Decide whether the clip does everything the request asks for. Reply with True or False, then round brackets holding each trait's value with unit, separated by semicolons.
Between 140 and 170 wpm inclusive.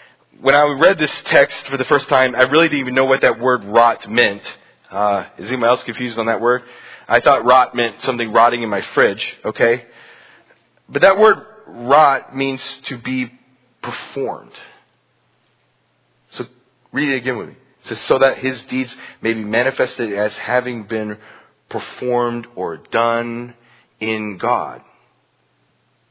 True (155 wpm)